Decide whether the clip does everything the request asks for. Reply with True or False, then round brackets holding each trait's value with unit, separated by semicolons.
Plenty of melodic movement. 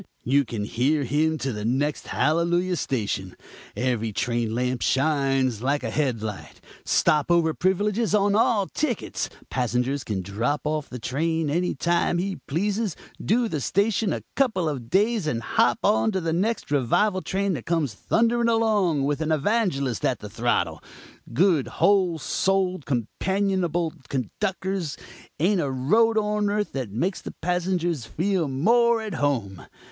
True (6.9 semitones)